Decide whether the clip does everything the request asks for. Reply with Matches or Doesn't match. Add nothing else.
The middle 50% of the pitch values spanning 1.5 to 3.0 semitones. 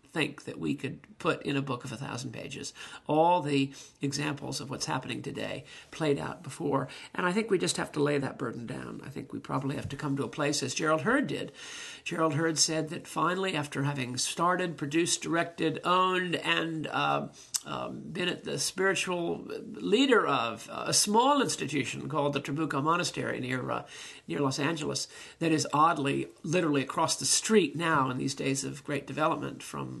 Doesn't match